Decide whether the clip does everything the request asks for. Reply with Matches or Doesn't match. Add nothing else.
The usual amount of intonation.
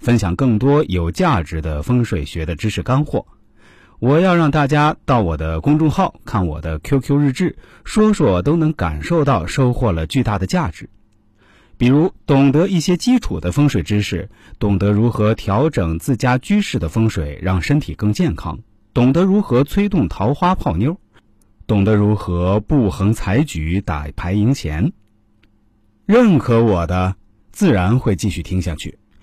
Doesn't match